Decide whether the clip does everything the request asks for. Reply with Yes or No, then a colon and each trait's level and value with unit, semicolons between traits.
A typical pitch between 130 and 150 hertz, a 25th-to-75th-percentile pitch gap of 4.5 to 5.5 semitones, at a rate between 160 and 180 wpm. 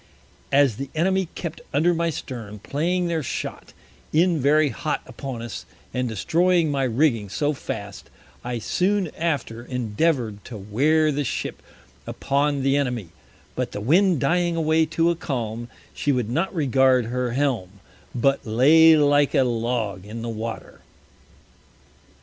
No: medium, 140 Hz; average, 5.2 semitones; average, 145 wpm